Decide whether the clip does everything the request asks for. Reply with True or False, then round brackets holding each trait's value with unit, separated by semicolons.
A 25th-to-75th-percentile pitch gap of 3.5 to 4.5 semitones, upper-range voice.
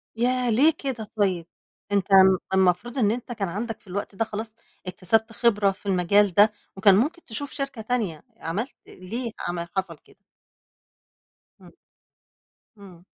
True (3.9 semitones; 210 Hz)